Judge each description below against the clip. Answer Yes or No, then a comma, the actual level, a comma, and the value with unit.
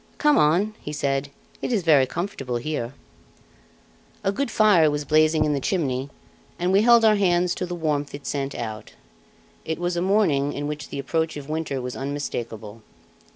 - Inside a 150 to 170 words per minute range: No, average, 180 wpm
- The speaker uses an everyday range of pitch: Yes, average, 4.4 semitones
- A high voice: No, medium, 155 Hz